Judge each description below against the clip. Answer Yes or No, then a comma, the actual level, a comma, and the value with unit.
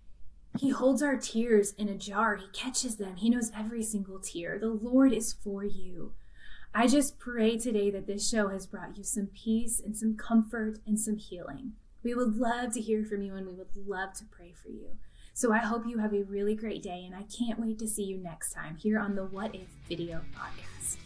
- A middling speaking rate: No, fast, 220 wpm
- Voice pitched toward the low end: No, high, 215 Hz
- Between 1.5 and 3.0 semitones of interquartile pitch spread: Yes, narrow, 2.6 semitones